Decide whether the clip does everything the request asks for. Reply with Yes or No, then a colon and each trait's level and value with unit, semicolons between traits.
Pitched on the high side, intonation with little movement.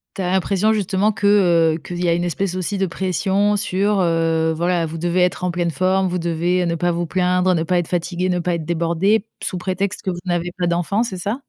No: medium, 180 Hz; narrow, 1.9 semitones